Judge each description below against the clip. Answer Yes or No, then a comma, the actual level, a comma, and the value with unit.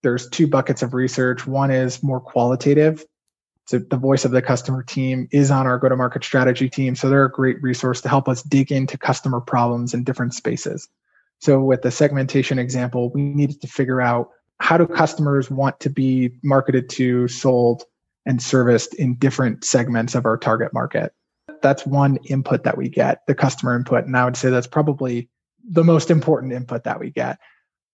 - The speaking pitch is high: No, low, 130 Hz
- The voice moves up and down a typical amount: No, narrow, 1.8 semitones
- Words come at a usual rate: Yes, average, 190 wpm